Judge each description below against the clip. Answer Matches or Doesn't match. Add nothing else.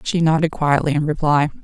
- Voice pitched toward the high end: Doesn't match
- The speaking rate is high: Doesn't match